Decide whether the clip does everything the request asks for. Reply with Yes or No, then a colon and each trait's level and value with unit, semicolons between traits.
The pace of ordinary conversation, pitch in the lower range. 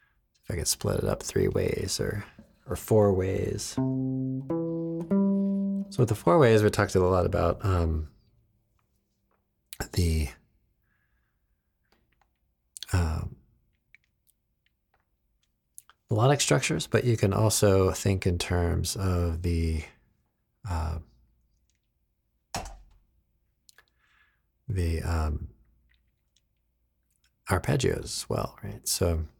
No: slow, 90 wpm; very low, 95 Hz